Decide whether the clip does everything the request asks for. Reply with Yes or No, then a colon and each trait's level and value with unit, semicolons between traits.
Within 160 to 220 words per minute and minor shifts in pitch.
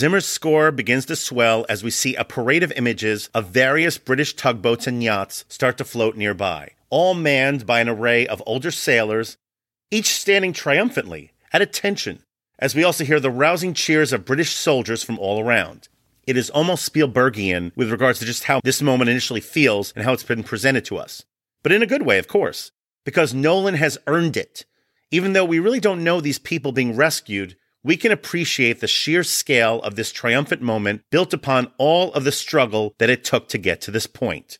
No: average, 200 wpm; average, 5.3 semitones